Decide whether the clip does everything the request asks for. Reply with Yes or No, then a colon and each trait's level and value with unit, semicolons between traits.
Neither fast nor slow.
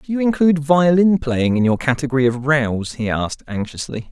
Yes: average, 190 wpm